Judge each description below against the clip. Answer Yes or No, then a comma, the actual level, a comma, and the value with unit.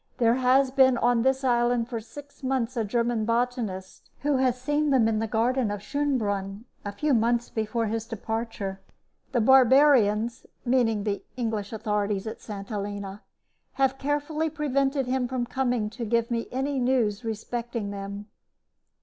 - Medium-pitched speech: No, high, 235 Hz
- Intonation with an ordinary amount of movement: Yes, average, 3.4 semitones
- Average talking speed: Yes, average, 155 wpm